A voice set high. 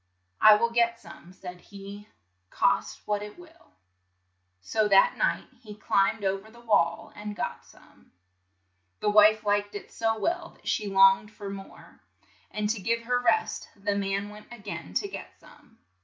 Yes: high, 210 Hz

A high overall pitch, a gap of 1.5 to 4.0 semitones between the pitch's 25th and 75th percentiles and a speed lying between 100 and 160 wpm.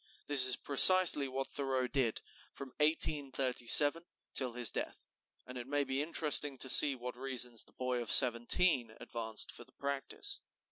No: low, 135 Hz; average, 2.7 semitones; average, 155 wpm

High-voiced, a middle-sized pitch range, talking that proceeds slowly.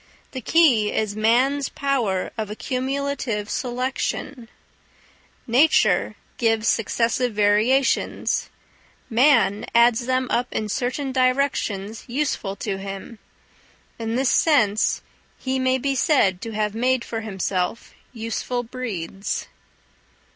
Yes: high, 235 Hz; average, 3.4 semitones; slow, 105 wpm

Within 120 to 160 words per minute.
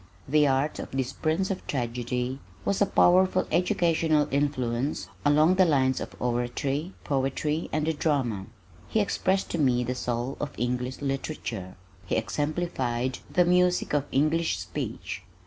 Yes: average, 145 wpm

